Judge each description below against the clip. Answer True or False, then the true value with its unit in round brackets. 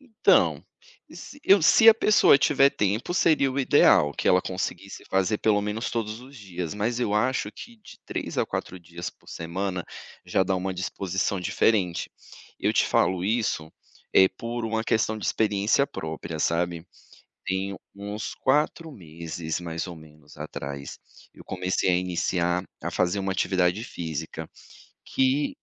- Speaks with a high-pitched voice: False (95 Hz)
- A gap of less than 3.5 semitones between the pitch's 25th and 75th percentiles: False (4.7 semitones)